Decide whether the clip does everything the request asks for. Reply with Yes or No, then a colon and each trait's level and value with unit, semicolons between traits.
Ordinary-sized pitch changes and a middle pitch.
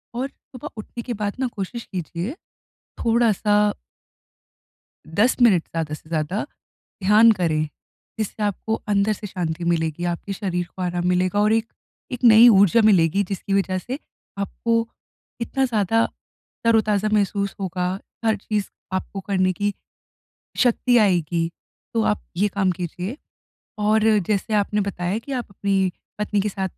No: average, 3.2 semitones; high, 200 Hz